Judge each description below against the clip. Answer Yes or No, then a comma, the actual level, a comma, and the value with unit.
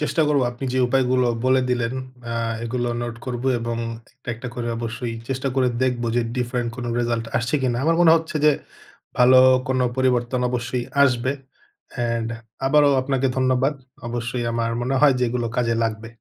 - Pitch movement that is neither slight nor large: No, narrow, 1.7 semitones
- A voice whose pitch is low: Yes, low, 125 Hz